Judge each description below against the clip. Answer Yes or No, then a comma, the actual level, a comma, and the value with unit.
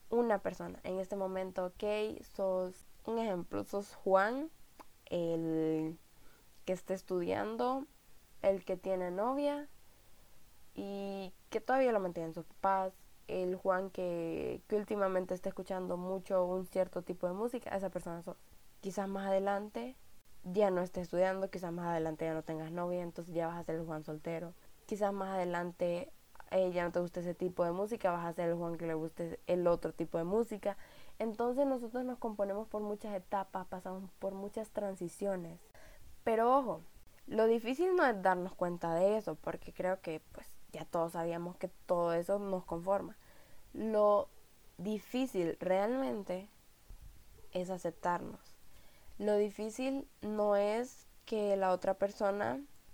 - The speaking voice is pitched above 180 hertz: Yes, high, 190 Hz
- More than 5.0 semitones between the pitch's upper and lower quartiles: No, average, 3.0 semitones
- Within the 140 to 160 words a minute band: Yes, average, 155 wpm